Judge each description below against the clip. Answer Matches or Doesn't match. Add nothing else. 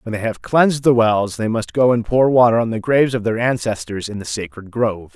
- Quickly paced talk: Matches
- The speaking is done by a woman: Doesn't match